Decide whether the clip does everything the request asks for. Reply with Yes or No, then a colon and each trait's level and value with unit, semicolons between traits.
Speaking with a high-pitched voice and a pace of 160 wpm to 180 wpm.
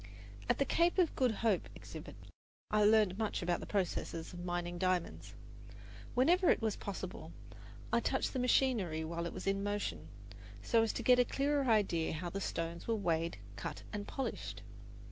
Yes: high, 205 Hz; average, 175 wpm